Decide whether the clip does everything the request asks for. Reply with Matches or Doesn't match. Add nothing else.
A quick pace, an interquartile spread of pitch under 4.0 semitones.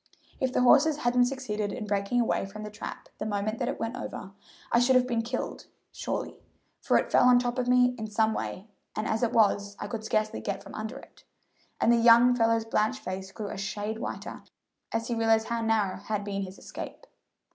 Matches